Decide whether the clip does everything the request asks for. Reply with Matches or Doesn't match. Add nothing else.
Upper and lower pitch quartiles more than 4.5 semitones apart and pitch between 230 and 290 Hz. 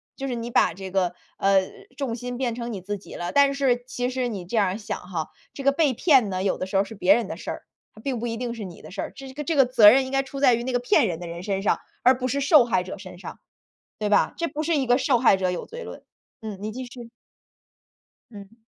Matches